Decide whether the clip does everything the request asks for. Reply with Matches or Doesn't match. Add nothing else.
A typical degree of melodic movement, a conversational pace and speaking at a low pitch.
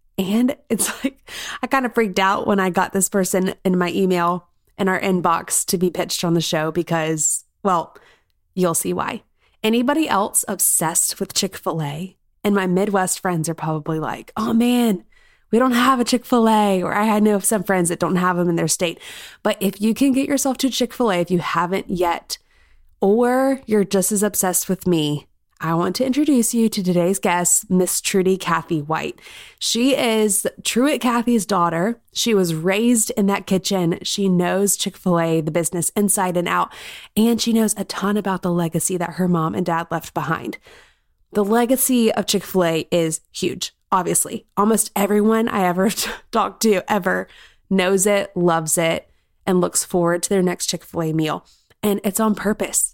Doesn't match